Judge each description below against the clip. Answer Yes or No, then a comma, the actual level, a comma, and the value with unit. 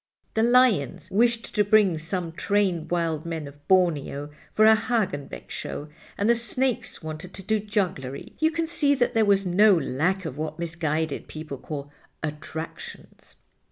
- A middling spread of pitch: No, wide, 5.7 semitones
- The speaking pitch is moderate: Yes, medium, 180 Hz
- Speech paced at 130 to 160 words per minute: Yes, average, 155 wpm